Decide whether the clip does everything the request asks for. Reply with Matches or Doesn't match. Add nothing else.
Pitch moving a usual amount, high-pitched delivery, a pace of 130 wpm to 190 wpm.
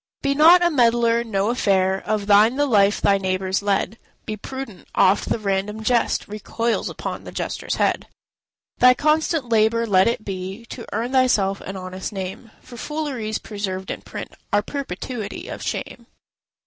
Matches